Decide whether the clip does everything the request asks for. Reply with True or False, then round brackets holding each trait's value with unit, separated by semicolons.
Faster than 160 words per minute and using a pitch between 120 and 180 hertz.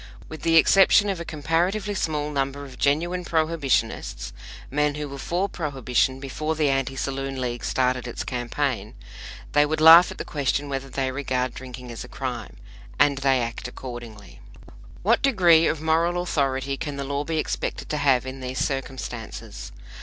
True (170 wpm; 140 Hz)